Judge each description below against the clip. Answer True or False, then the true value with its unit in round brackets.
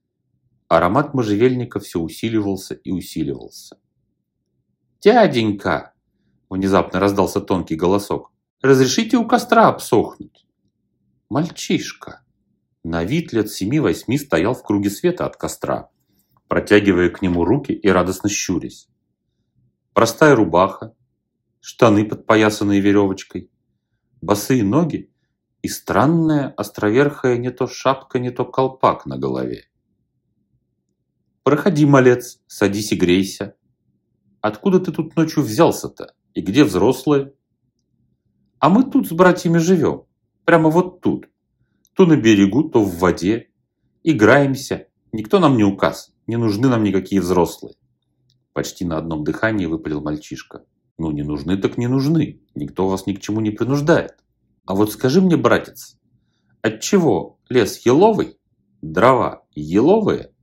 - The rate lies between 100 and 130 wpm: True (115 wpm)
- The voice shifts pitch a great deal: True (6.3 semitones)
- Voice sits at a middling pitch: False (110 Hz)